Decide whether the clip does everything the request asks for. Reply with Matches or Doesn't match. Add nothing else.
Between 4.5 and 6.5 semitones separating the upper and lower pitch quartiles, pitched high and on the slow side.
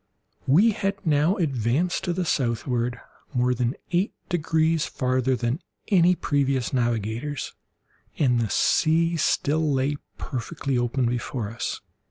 Doesn't match